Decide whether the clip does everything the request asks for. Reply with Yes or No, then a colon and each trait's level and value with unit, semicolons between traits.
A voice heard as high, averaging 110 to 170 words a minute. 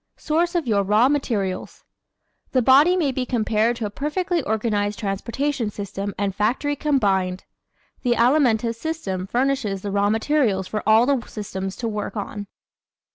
Yes: high, 225 Hz; average, 155 wpm